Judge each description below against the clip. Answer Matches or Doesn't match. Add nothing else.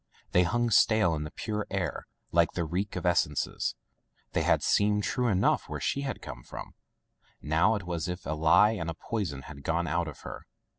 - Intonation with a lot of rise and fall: Doesn't match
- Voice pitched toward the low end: Matches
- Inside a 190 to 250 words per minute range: Matches